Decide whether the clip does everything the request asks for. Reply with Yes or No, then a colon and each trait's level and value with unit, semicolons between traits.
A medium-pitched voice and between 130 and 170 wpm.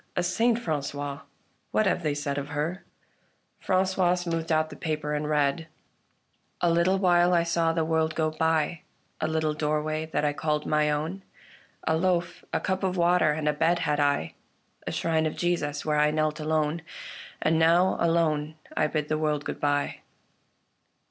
No: medium, 160 Hz; average, 180 wpm